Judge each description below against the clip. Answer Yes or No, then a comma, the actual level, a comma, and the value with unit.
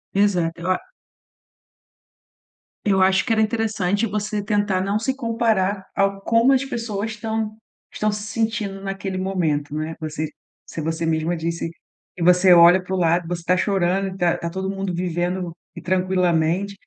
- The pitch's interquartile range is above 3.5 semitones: No, average, 3.2 semitones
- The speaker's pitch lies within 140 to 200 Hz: Yes, high, 190 Hz